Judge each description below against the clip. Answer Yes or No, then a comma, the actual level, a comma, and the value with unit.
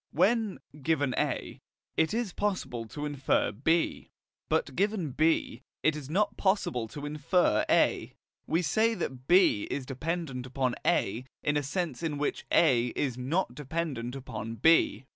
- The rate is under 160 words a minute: Yes, average, 150 wpm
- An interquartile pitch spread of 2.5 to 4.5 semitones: No, average, 5.2 semitones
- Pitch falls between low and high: Yes, medium, 150 Hz